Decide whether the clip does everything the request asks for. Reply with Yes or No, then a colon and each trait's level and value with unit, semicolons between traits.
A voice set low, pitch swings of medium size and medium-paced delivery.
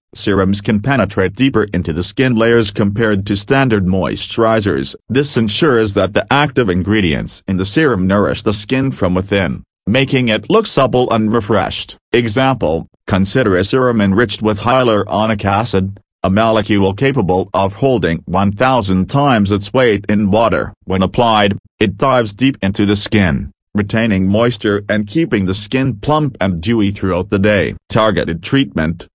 Yes: low, 105 Hz; average, 4.0 semitones; average, 150 wpm